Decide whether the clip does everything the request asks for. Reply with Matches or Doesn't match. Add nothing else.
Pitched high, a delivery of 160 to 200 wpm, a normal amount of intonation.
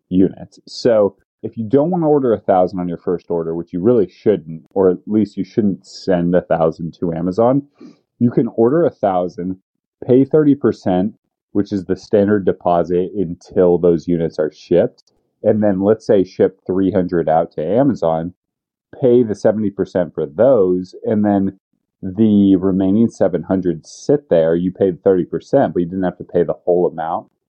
Doesn't match